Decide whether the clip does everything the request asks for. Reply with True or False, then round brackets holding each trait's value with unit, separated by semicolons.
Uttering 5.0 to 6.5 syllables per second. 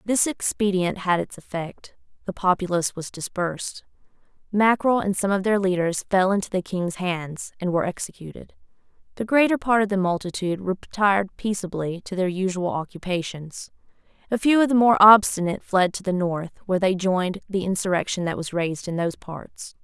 True (5.4 syllables/s)